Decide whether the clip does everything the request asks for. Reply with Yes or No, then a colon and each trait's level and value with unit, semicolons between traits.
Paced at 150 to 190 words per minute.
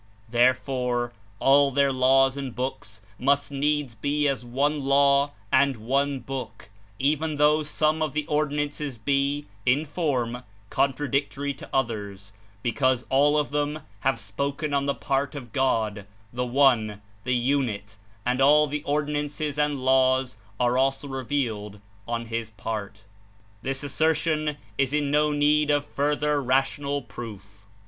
No: average, 140 wpm